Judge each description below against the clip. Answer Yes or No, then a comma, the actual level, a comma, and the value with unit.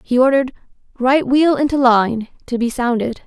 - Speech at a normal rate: Yes, average, 165 wpm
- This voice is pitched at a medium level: No, very high, 255 Hz